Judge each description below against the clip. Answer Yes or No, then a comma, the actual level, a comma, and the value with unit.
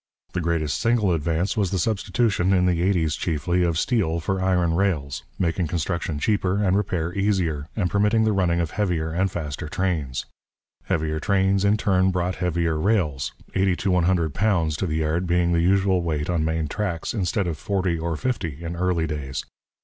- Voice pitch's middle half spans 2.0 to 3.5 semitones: Yes, average, 3.1 semitones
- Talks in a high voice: No, very low, 90 Hz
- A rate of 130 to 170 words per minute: No, average, 185 wpm